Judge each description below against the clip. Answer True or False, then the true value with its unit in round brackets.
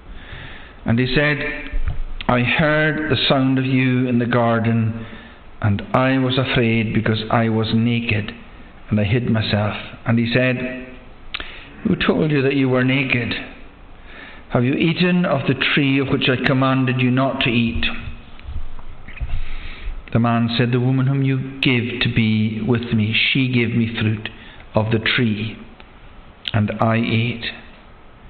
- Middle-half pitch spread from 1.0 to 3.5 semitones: True (2.9 semitones)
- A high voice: False (120 Hz)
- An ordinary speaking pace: True (150 wpm)